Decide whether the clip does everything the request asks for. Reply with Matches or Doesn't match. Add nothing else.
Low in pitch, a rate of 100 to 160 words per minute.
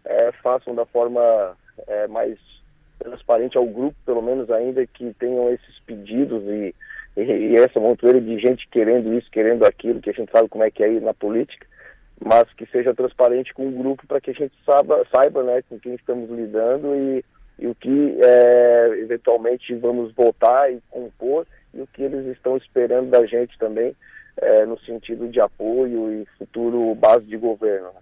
Doesn't match